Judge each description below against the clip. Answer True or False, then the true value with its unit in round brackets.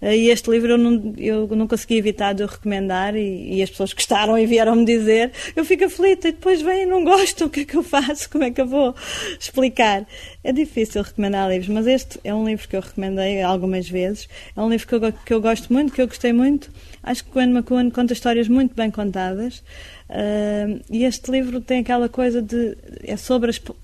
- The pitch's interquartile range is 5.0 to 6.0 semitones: False (3.7 semitones)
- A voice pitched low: False (235 Hz)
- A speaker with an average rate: False (220 wpm)